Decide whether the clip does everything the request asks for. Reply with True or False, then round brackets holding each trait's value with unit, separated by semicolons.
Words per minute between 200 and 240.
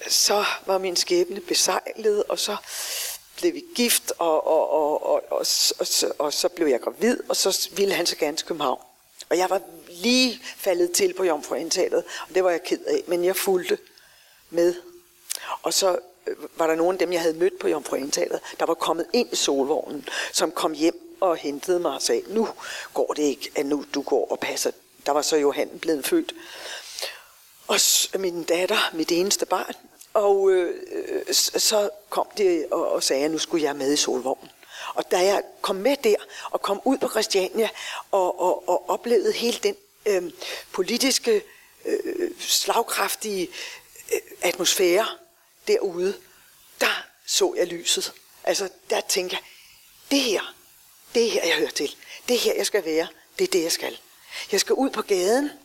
False (180 wpm)